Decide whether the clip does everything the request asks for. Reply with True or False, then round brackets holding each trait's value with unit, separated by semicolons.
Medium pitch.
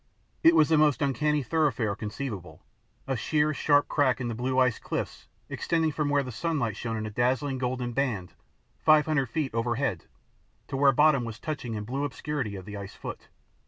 False (130 Hz)